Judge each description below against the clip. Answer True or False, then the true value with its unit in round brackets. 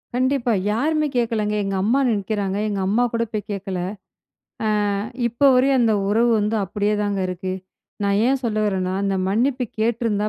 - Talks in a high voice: True (215 Hz)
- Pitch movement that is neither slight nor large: True (3.2 semitones)